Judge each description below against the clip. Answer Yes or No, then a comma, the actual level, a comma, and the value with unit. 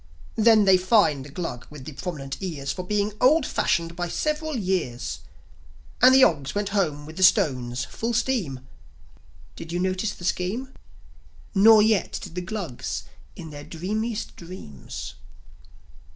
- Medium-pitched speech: Yes, medium, 180 Hz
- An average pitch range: No, wide, 6.4 semitones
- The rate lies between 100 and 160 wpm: Yes, average, 150 wpm